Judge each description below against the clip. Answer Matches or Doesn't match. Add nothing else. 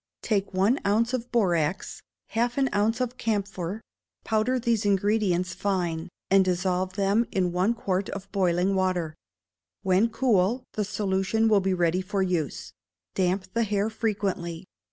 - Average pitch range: Matches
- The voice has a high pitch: Matches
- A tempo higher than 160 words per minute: Doesn't match